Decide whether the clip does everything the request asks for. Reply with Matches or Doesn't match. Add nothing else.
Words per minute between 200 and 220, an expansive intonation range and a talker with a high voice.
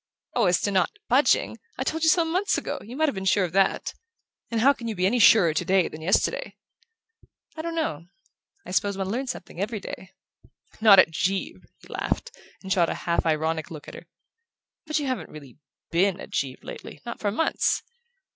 Matches